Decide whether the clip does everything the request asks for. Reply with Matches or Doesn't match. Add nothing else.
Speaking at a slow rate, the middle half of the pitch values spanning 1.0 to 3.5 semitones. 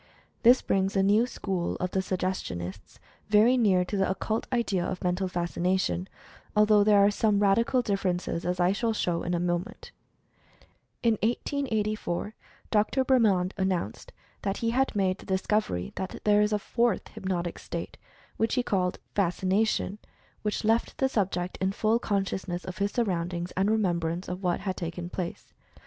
Doesn't match